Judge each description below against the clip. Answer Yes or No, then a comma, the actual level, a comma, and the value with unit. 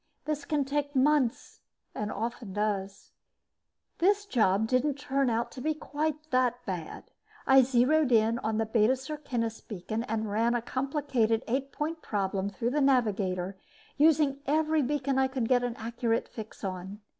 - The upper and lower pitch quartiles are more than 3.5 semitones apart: Yes, average, 4.5 semitones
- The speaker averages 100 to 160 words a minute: Yes, average, 155 wpm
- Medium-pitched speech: No, high, 245 Hz